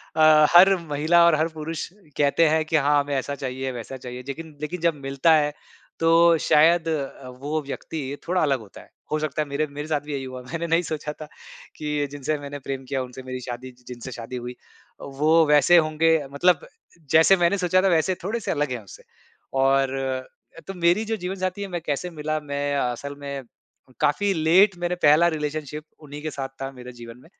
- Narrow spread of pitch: No, average, 3.3 semitones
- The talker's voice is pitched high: No, medium, 150 Hz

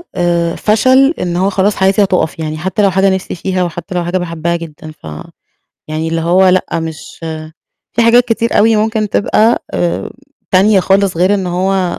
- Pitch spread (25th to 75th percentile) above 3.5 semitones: No, average, 3.2 semitones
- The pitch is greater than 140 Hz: Yes, medium, 185 Hz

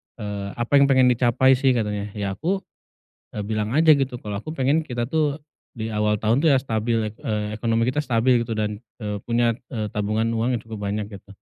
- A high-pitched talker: No, low, 115 Hz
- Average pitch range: Yes, average, 3.5 semitones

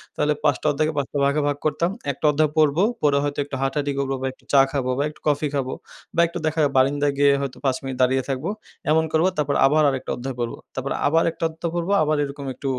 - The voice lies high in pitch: No, medium, 145 Hz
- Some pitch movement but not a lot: No, narrow, 2.3 semitones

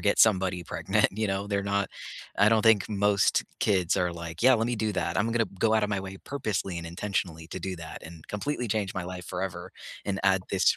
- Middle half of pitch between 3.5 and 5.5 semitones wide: No, average, 3.1 semitones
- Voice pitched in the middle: No, very low, 95 Hz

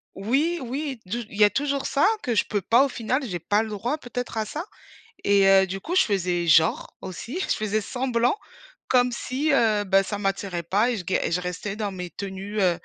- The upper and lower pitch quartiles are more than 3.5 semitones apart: Yes, average, 4.6 semitones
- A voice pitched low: No, high, 215 Hz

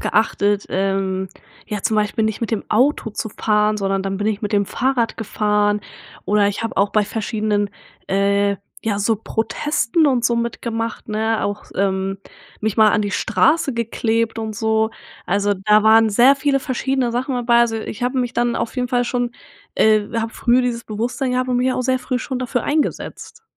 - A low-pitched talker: No, high, 220 Hz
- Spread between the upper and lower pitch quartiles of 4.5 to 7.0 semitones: No, average, 2.9 semitones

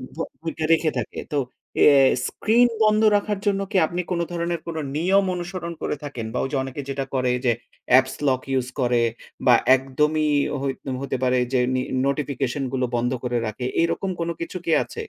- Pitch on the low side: No, medium, 145 Hz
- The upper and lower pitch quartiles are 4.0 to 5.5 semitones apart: Yes, average, 5.1 semitones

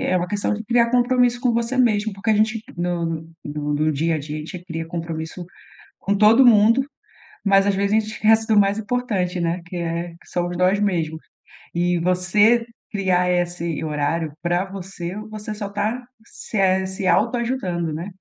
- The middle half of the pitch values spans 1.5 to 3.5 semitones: No, average, 4.1 semitones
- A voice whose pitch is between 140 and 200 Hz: Yes, high, 190 Hz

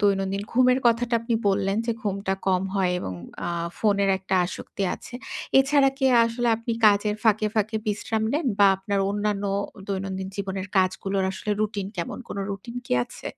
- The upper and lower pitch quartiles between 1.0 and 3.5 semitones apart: Yes, average, 2.9 semitones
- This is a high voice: Yes, high, 200 Hz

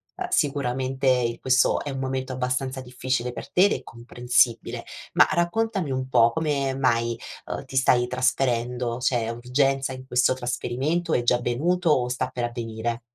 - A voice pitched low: Yes, low, 130 Hz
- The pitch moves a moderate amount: No, narrow, 1.9 semitones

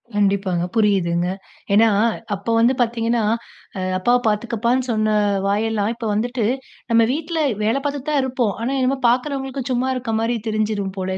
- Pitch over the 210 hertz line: Yes, high, 230 Hz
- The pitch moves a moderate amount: Yes, average, 3.4 semitones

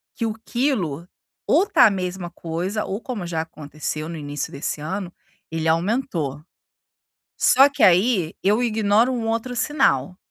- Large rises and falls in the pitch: Yes, wide, 6.2 semitones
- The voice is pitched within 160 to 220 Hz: Yes, high, 190 Hz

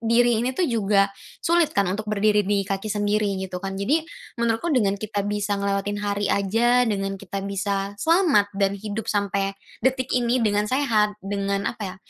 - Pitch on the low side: No, high, 205 Hz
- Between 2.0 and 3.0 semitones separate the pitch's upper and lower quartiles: Yes, narrow, 2.6 semitones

